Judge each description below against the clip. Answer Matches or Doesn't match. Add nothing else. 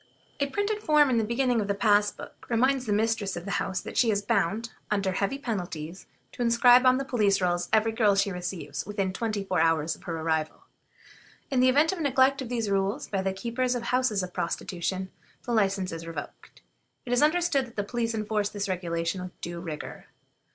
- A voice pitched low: Doesn't match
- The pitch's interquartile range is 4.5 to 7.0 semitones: Matches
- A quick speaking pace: Matches